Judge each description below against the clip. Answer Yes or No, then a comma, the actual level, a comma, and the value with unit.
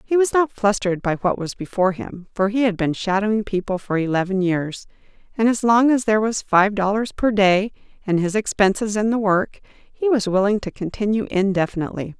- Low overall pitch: No, high, 205 Hz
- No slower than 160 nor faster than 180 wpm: No, average, 195 wpm